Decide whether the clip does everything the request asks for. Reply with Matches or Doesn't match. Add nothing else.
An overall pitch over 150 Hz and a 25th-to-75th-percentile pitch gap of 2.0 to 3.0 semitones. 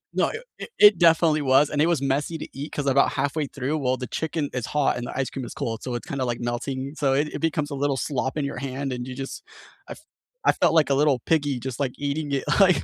Doesn't match